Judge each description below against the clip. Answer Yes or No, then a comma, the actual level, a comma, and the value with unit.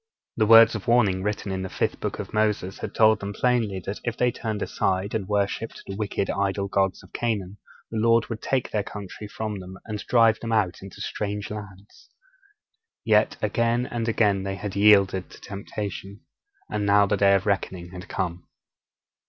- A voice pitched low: Yes, low, 105 Hz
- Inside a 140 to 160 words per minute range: No, average, 185 wpm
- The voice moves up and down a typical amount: No, narrow, 2.1 semitones